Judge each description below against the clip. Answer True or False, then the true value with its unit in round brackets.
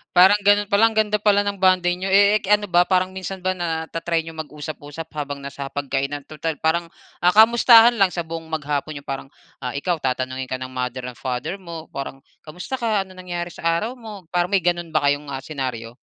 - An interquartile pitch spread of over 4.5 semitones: True (5.0 semitones)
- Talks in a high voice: False (165 Hz)